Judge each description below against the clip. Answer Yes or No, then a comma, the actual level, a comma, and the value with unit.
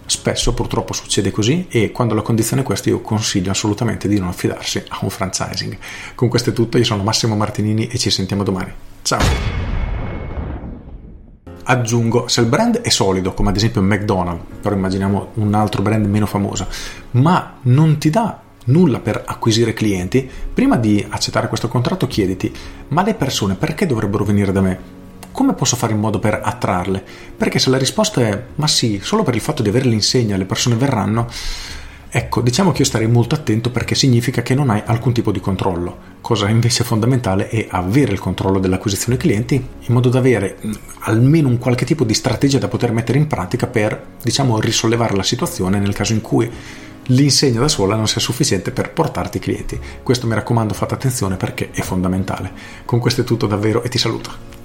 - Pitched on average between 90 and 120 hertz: Yes, low, 110 Hz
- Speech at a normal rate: No, fast, 190 wpm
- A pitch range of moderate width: Yes, average, 3.8 semitones